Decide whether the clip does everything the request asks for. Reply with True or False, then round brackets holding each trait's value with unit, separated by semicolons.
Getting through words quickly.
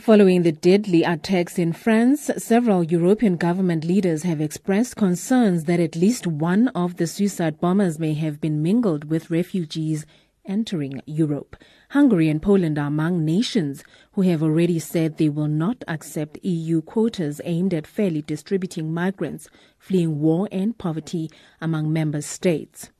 False (150 wpm)